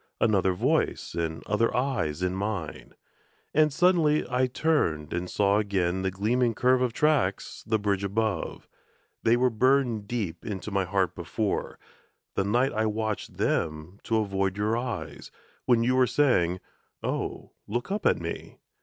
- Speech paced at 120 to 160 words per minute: Yes, average, 155 wpm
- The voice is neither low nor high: No, low, 105 Hz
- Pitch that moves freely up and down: No, average, 4.7 semitones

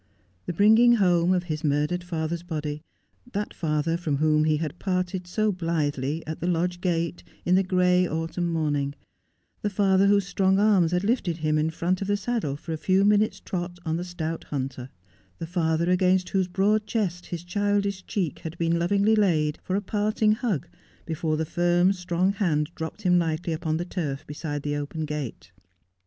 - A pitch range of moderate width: Yes, average, 3.3 semitones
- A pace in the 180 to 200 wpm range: Yes, average, 185 wpm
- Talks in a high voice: No, medium, 175 Hz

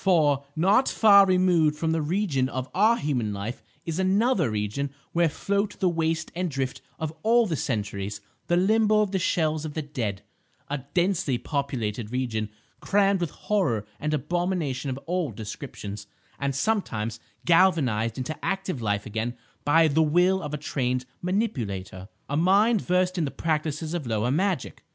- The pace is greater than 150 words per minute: Yes, average, 160 wpm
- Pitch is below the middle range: No, medium, 155 Hz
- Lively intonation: Yes, wide, 6.5 semitones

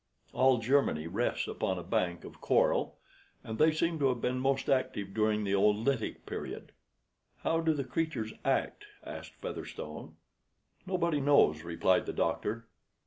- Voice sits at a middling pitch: No, low, 125 Hz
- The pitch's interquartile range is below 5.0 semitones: No, wide, 5.6 semitones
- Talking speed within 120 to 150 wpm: Yes, average, 145 wpm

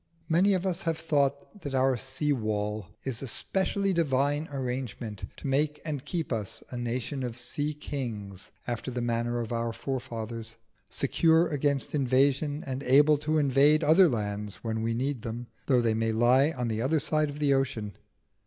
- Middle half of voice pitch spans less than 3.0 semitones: No, average, 4.2 semitones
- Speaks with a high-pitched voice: No, low, 135 Hz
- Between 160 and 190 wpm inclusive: Yes, average, 175 wpm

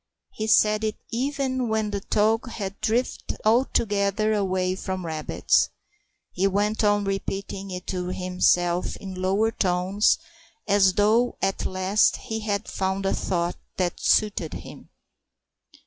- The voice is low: No, high, 200 Hz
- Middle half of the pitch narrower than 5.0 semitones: Yes, narrow, 2.6 semitones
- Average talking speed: No, slow, 130 wpm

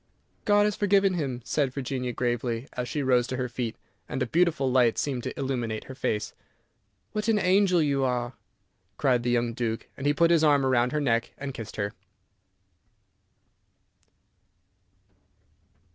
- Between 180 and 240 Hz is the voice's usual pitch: No, low, 130 Hz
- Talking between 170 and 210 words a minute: No, average, 160 wpm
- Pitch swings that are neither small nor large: Yes, average, 4.0 semitones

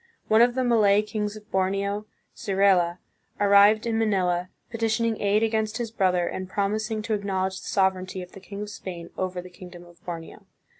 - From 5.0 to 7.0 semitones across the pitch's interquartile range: No, narrow, 2.6 semitones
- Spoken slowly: No, average, 185 wpm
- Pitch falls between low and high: No, high, 200 Hz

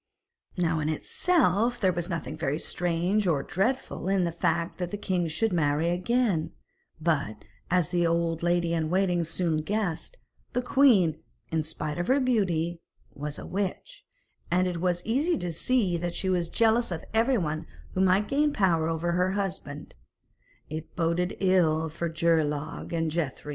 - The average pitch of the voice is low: No, medium, 175 Hz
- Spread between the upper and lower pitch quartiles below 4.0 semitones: Yes, average, 3.2 semitones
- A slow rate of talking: No, average, 165 wpm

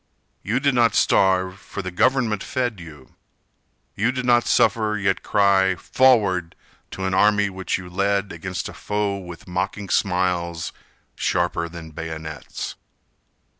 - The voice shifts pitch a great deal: No, average, 3.0 semitones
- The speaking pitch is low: Yes, very low, 95 Hz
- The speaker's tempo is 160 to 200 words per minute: No, slow, 135 wpm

